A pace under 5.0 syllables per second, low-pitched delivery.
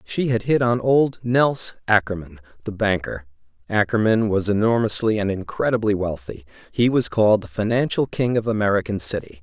No: 5.3 syllables/s; low, 105 Hz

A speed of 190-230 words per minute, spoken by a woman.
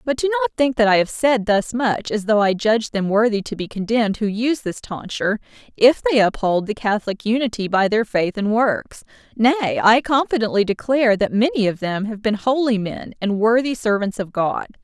Yes: fast, 205 wpm; female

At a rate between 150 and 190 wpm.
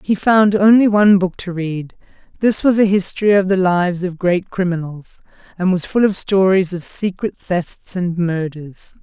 Yes: average, 180 wpm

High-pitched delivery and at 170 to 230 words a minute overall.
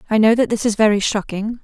No: high, 215 Hz; fast, 255 wpm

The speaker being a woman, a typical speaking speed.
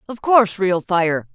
Yes: female; average, 180 wpm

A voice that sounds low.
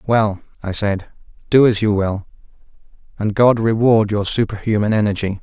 Yes: low, 105 Hz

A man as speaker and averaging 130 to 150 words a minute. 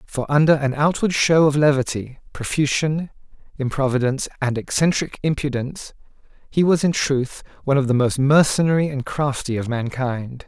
Yes: male; average, 145 wpm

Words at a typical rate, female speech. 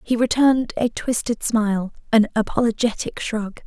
No: slow, 130 wpm; female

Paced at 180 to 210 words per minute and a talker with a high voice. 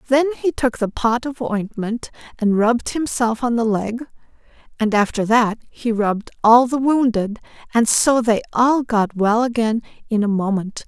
No: average, 170 wpm; high, 230 Hz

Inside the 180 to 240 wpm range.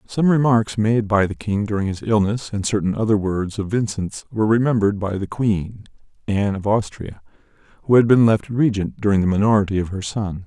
Yes: average, 195 wpm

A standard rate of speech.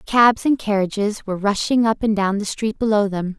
No: fast, 210 wpm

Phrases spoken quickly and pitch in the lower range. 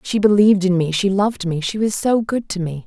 No: fast, 230 wpm; high, 195 Hz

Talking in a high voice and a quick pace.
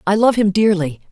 Yes: high, 195 Hz; fast, 215 wpm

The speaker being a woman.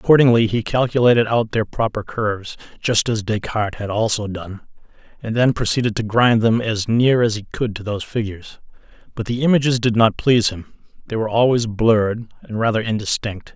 No: male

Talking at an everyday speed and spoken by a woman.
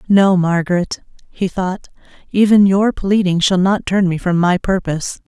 Yes: average, 160 wpm; female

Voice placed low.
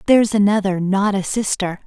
No: high, 200 Hz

